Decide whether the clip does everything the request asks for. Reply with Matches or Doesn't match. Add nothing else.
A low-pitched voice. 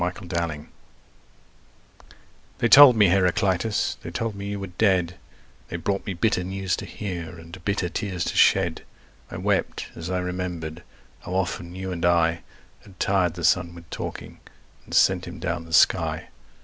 Matches